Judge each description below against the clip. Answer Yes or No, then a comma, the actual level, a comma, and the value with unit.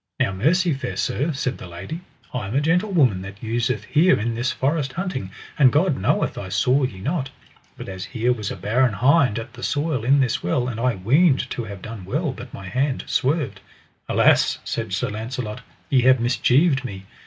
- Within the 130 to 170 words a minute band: No, average, 200 wpm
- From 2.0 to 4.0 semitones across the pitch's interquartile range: No, average, 4.9 semitones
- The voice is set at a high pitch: No, low, 125 Hz